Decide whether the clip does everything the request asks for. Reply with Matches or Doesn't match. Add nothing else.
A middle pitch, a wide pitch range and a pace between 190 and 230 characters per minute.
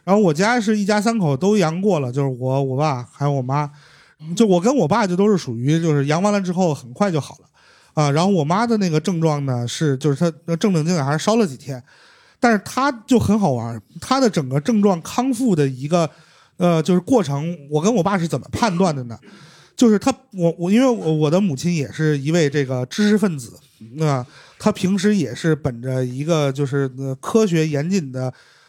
Doesn't match